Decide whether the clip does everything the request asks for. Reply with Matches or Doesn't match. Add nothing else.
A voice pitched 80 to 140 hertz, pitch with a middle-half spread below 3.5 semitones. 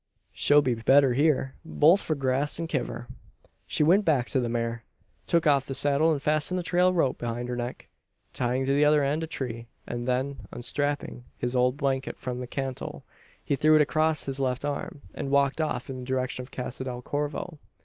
Matches